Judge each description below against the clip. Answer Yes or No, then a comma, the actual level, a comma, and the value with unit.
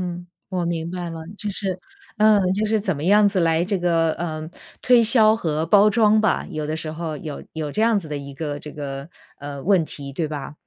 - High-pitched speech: No, medium, 170 Hz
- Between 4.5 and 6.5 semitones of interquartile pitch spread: Yes, average, 4.9 semitones